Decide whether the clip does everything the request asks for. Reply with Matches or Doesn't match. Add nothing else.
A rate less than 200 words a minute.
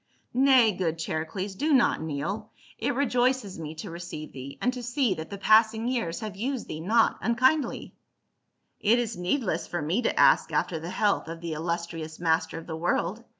Doesn't match